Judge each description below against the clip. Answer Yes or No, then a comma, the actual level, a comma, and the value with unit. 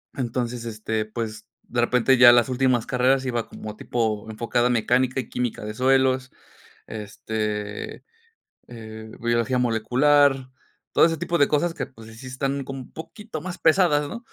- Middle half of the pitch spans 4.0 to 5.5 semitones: No, average, 3.2 semitones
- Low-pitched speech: Yes, low, 125 Hz